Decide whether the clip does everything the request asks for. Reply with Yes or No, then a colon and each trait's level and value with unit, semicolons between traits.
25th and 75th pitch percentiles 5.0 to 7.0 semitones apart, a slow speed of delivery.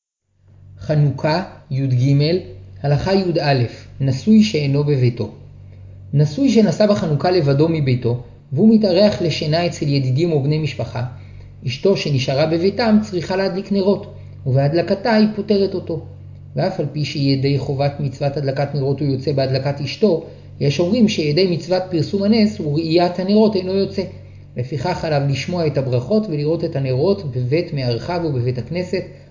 No: wide, 5.4 semitones; average, 130 wpm